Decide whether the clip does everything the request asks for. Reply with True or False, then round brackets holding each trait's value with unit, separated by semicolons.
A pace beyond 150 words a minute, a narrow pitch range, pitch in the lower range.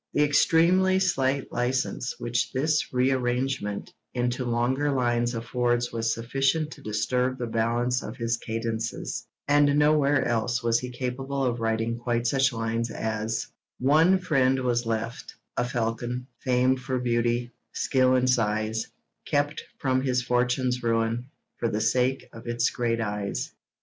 False (140 wpm; 2.3 semitones; 125 Hz)